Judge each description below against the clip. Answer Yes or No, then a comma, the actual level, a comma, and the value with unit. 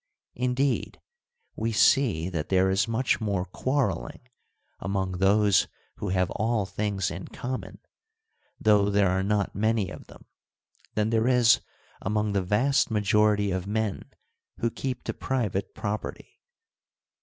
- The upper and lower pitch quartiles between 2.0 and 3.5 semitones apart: Yes, average, 2.9 semitones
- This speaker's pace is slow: Yes, slow, 130 wpm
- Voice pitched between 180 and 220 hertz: No, low, 105 Hz